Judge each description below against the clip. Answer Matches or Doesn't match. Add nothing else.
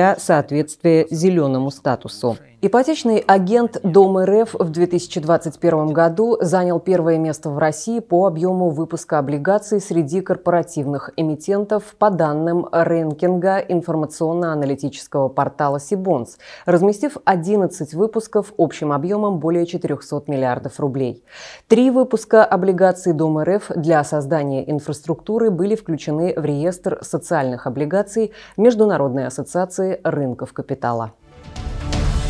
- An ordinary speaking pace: Doesn't match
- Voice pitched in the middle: Matches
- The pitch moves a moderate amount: Matches